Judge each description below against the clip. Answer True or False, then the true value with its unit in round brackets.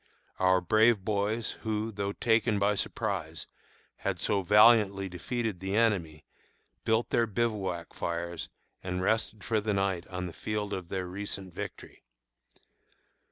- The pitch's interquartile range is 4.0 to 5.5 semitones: False (3.0 semitones)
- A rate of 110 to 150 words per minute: True (135 wpm)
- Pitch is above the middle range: False (100 Hz)